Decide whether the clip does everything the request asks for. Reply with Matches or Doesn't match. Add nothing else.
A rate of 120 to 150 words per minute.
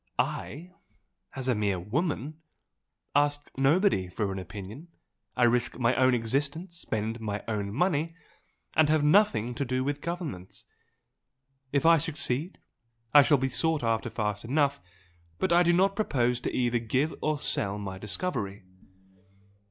Matches